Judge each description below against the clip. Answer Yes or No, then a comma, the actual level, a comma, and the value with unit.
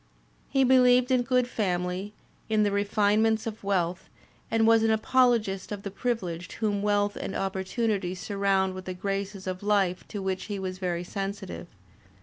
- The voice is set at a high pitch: Yes, high, 200 Hz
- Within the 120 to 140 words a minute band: No, average, 165 wpm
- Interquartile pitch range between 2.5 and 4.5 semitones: Yes, average, 2.8 semitones